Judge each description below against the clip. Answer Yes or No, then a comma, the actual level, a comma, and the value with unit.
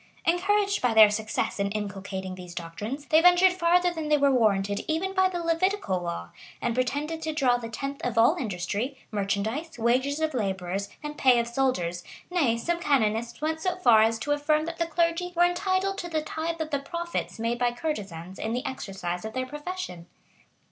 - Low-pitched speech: No, very high, 265 Hz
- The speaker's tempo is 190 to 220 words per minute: Yes, average, 195 wpm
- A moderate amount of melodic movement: No, wide, 7.7 semitones